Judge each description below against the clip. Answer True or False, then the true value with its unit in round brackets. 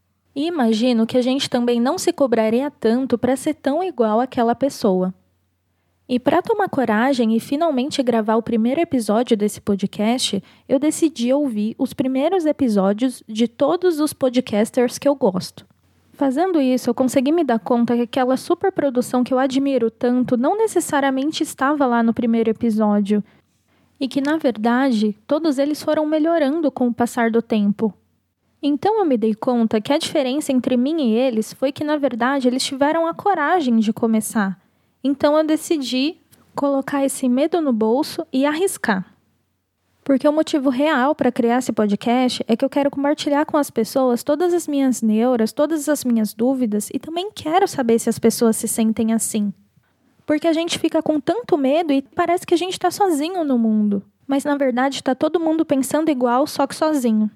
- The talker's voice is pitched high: True (265 Hz)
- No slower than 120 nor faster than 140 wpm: False (175 wpm)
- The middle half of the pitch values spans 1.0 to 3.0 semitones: False (4.4 semitones)